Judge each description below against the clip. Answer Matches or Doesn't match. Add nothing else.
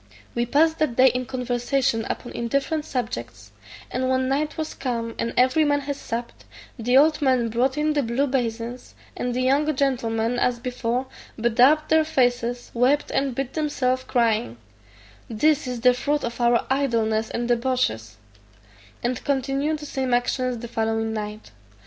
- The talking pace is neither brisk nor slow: Matches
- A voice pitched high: Matches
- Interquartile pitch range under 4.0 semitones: Matches